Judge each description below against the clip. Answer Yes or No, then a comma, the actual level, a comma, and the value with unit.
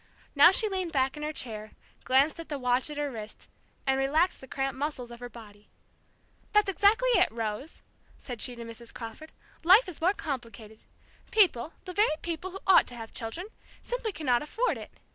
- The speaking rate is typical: Yes, average, 190 wpm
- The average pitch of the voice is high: Yes, very high, 280 Hz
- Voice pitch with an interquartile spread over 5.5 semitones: Yes, wide, 7.1 semitones